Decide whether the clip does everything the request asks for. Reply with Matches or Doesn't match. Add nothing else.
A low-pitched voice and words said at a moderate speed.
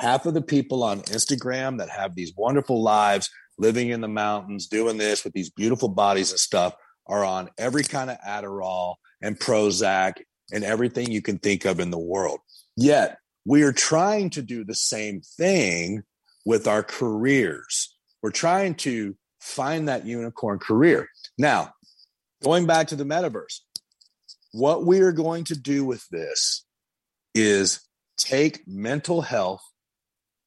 Matches